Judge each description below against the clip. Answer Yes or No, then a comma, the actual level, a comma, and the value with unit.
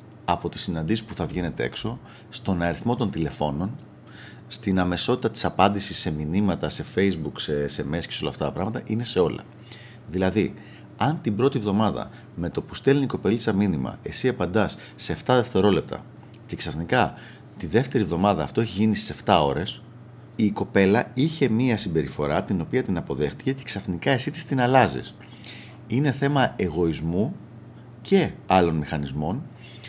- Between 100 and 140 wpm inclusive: No, average, 160 wpm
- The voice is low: Yes, low, 100 Hz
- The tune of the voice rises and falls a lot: Yes, wide, 5.8 semitones